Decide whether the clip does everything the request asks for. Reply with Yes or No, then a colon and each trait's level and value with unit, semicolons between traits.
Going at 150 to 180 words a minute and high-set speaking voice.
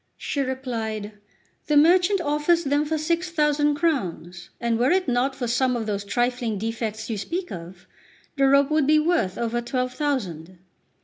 Yes: average, 170 wpm; very high, 260 Hz